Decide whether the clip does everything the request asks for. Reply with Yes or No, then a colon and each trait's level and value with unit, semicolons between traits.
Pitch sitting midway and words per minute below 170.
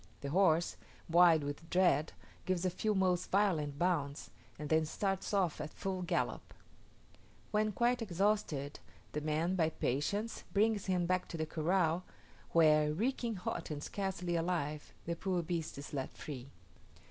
Yes: medium, 175 Hz; average, 150 wpm